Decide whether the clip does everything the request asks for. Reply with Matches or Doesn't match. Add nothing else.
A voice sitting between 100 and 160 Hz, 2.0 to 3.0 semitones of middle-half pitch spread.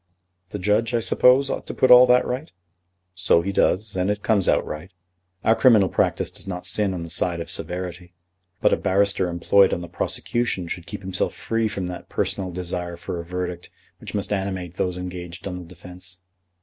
Doesn't match